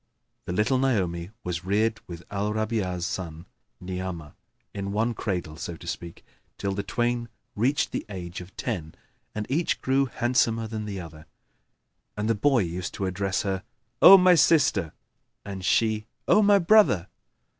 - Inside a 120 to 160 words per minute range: Yes, average, 155 wpm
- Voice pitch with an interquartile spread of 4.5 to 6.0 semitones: Yes, average, 4.8 semitones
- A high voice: No, low, 100 Hz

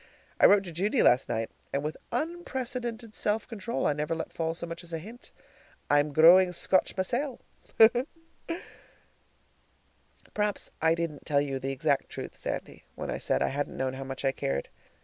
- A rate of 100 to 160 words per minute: No, average, 170 wpm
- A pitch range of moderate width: No, wide, 6.7 semitones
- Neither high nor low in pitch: Yes, medium, 165 Hz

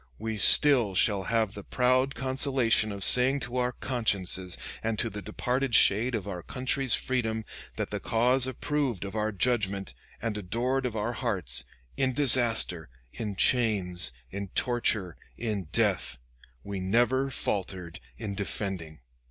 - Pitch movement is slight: No, average, 4.3 semitones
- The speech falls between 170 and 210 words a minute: No, average, 145 wpm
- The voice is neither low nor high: No, low, 110 Hz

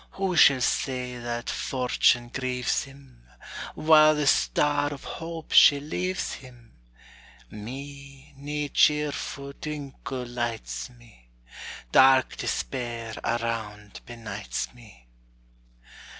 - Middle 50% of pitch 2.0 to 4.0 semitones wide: Yes, average, 3.5 semitones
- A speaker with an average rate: No, slow, 95 wpm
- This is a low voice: Yes, low, 130 Hz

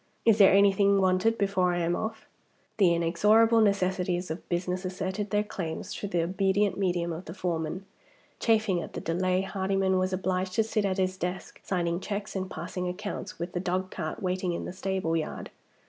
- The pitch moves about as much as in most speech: No, narrow, 2.0 semitones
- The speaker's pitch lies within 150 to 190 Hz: Yes, medium, 185 Hz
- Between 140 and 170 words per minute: No, average, 180 wpm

